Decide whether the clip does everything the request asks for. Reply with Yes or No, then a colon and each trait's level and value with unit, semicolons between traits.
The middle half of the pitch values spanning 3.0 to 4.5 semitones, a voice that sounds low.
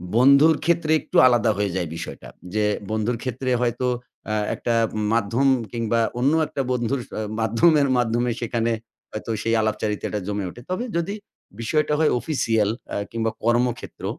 Yes: average, 3.6 semitones; low, 120 Hz